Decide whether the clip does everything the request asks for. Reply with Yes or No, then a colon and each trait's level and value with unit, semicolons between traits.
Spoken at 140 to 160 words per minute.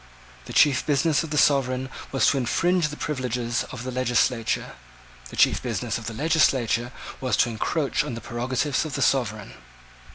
No: average, 170 wpm